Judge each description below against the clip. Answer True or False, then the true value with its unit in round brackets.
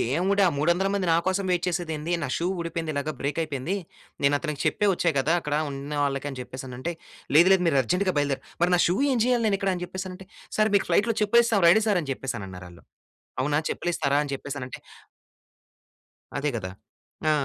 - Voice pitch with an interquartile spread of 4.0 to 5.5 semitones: True (5.0 semitones)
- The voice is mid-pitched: True (165 Hz)